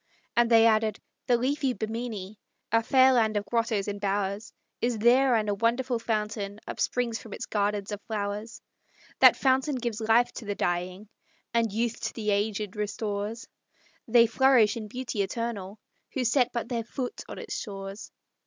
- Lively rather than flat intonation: No, narrow, 2.6 semitones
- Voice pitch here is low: No, high, 225 Hz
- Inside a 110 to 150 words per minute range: No, average, 165 wpm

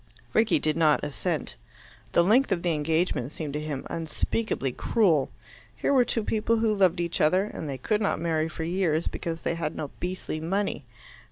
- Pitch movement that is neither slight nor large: Yes, average, 4.3 semitones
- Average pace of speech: Yes, average, 185 wpm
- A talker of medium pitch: Yes, medium, 170 Hz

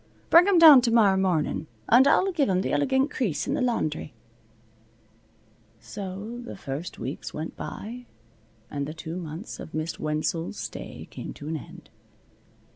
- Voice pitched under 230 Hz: Yes, high, 190 Hz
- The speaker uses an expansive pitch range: Yes, wide, 7.9 semitones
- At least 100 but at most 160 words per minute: Yes, average, 155 wpm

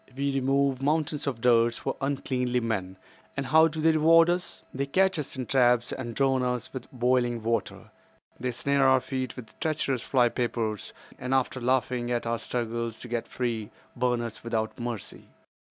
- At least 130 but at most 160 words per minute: No, average, 175 wpm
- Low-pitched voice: Yes, low, 125 Hz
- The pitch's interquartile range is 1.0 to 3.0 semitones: Yes, narrow, 2.5 semitones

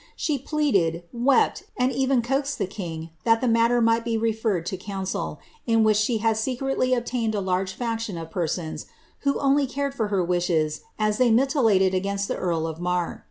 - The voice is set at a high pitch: Yes, high, 220 Hz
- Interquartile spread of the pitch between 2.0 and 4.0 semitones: No, average, 5.3 semitones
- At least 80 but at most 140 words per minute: No, average, 190 wpm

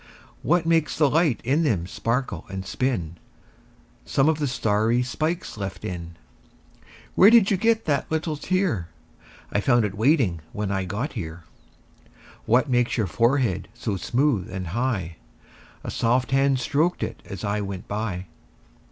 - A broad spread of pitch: Yes, wide, 7.2 semitones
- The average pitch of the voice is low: Yes, low, 120 Hz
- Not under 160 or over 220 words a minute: No, average, 150 wpm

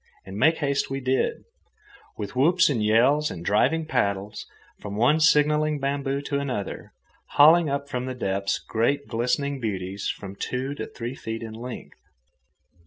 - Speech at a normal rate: Yes, average, 155 wpm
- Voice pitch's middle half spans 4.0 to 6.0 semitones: Yes, average, 4.8 semitones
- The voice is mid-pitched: No, low, 130 Hz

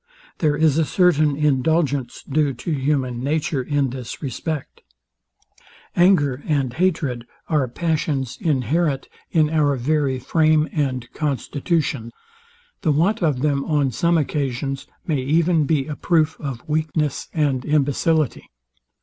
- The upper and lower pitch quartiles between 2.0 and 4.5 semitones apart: Yes, average, 2.9 semitones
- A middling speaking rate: No, slow, 125 wpm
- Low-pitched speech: No, medium, 150 Hz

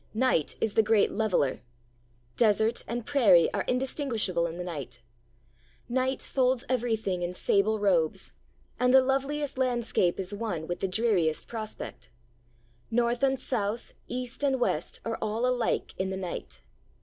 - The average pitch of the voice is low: No, high, 220 Hz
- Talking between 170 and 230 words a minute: No, average, 145 wpm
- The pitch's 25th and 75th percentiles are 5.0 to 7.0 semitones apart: Yes, wide, 5.4 semitones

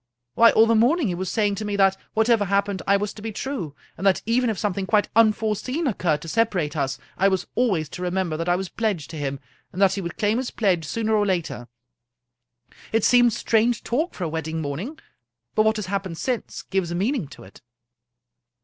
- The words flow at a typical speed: No, fast, 220 wpm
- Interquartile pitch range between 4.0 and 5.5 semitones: Yes, average, 4.3 semitones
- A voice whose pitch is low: No, high, 200 Hz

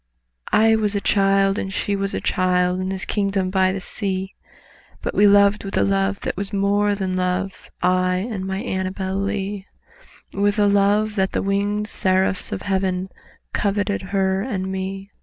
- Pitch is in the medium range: No, high, 195 Hz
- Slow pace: No, average, 175 wpm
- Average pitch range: No, narrow, 1.2 semitones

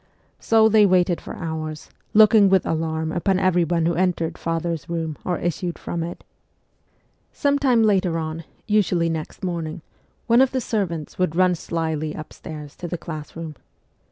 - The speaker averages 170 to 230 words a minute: No, average, 155 wpm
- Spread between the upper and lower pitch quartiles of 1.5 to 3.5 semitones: Yes, average, 2.9 semitones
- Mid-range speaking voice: Yes, medium, 170 Hz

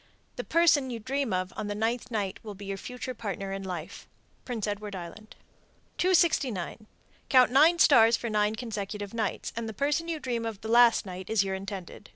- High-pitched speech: Yes, high, 220 Hz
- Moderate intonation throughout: Yes, average, 4.0 semitones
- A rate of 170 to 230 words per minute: Yes, average, 190 wpm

